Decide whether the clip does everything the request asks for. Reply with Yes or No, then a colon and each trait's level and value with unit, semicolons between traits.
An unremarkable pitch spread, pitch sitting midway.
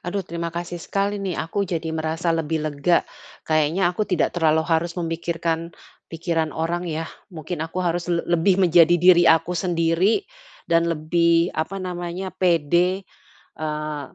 No: narrow, 1.7 semitones; medium, 170 Hz